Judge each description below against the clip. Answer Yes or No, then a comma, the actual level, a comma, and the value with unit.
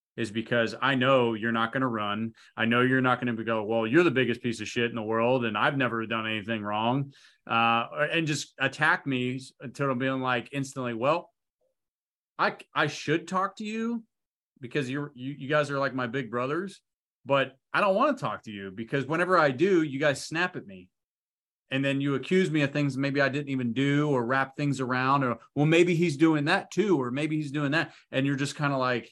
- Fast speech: Yes, fast, 225 wpm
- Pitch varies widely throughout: No, average, 3.8 semitones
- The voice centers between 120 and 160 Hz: Yes, low, 135 Hz